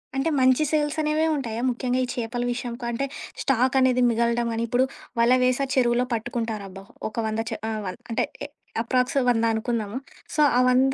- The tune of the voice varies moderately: No, narrow, 2.0 semitones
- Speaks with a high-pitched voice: Yes, high, 245 Hz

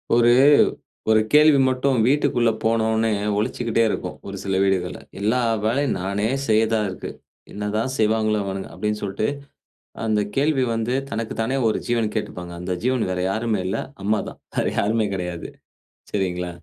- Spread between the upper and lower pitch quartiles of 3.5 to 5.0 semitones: No, average, 2.9 semitones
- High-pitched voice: No, low, 110 Hz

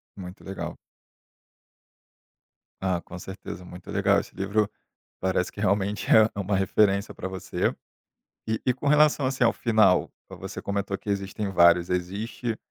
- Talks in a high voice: No, low, 100 Hz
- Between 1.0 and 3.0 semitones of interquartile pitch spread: Yes, narrow, 2.6 semitones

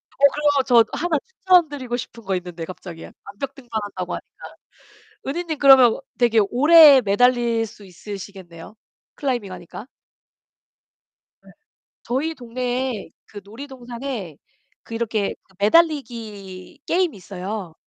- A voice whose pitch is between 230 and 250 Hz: Yes, high, 235 Hz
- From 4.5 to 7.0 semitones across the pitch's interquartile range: Yes, wide, 5.4 semitones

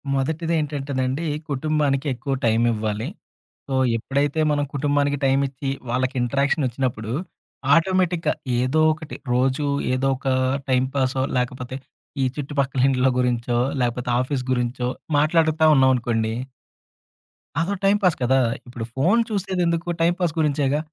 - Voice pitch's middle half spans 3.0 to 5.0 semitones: Yes, average, 3.3 semitones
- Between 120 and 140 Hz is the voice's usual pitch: Yes, low, 135 Hz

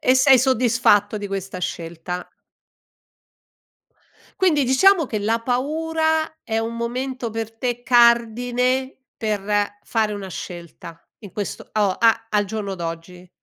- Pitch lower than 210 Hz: No, high, 225 Hz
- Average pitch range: Yes, average, 4.0 semitones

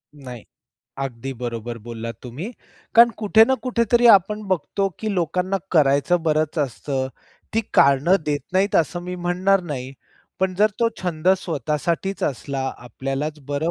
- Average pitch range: No, wide, 5.8 semitones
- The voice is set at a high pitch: No, medium, 160 Hz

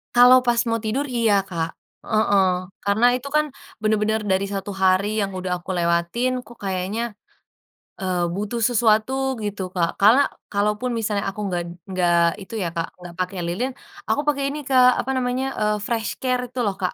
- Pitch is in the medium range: No, high, 210 Hz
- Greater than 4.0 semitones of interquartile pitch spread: Yes, average, 4.4 semitones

